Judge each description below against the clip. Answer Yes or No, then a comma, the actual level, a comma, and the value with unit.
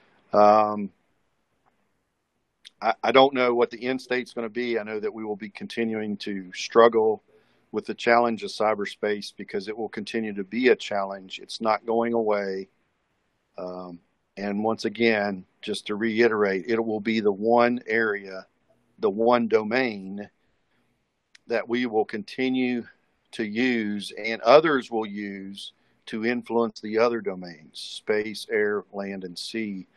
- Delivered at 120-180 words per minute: Yes, average, 150 wpm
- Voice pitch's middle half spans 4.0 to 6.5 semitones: No, narrow, 2.4 semitones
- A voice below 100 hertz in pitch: No, low, 110 Hz